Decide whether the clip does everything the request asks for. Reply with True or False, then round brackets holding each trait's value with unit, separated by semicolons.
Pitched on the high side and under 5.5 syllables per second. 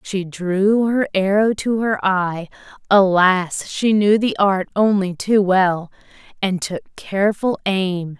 True (195 Hz; 3.6 syllables/s)